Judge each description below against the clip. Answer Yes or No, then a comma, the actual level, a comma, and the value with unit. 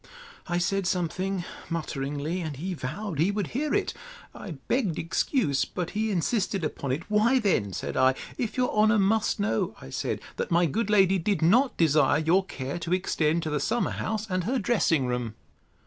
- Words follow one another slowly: No, average, 185 wpm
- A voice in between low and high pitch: Yes, medium, 180 Hz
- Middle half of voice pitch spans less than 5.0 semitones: No, wide, 5.4 semitones